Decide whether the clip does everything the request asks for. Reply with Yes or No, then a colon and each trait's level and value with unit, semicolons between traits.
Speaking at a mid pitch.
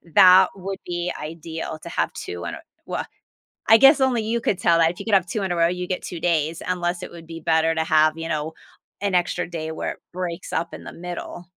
Yes: medium, 175 Hz